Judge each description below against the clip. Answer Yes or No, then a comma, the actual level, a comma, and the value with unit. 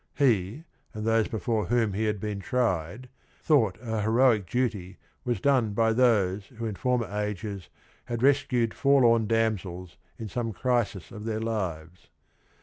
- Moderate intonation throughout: Yes, average, 3.2 semitones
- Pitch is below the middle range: Yes, low, 110 Hz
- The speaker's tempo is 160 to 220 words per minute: No, average, 145 wpm